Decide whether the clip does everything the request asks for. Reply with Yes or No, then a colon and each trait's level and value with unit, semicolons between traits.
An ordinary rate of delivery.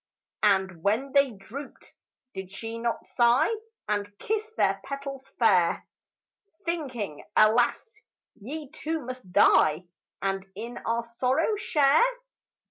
No: slow, 115 wpm